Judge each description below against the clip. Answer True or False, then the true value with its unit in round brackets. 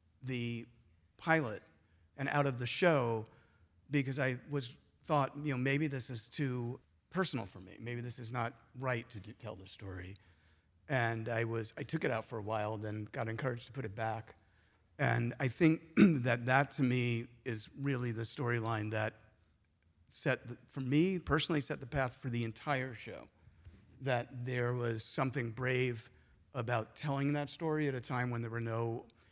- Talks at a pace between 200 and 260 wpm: False (175 wpm)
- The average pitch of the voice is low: True (120 Hz)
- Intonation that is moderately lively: True (3.6 semitones)